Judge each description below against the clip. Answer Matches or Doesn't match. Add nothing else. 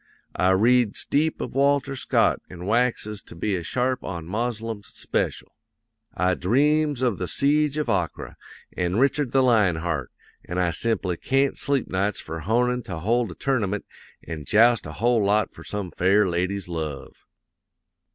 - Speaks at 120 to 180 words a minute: Matches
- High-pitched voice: Doesn't match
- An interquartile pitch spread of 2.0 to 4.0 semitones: Doesn't match